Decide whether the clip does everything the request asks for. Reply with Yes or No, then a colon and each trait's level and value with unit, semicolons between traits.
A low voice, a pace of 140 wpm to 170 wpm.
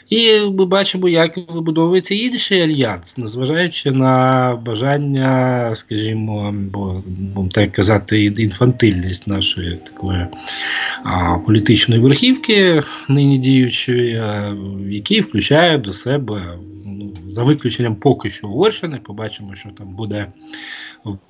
No: low, 115 Hz; slow, 105 wpm